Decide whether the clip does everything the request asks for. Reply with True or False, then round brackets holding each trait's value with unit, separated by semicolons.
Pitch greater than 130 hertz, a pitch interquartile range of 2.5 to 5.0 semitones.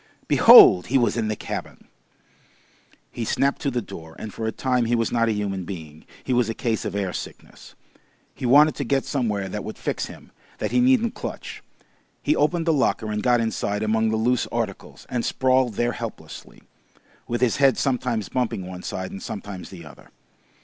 False (115 Hz; 3.8 semitones)